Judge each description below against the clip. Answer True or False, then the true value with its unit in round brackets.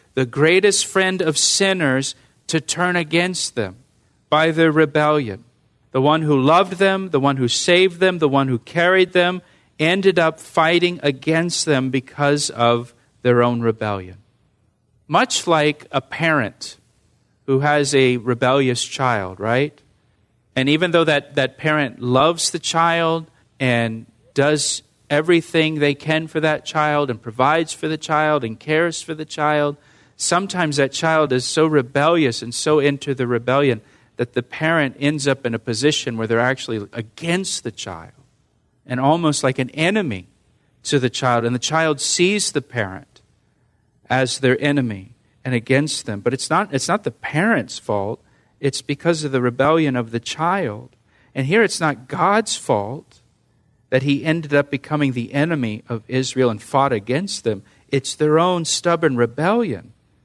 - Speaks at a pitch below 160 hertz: True (140 Hz)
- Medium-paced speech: True (160 wpm)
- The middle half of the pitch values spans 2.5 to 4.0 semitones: False (4.6 semitones)